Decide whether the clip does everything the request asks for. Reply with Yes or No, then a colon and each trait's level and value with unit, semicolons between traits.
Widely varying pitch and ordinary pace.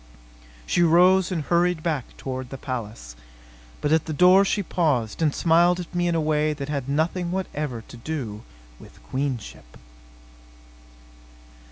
No: average, 4.8 semitones; average, 150 wpm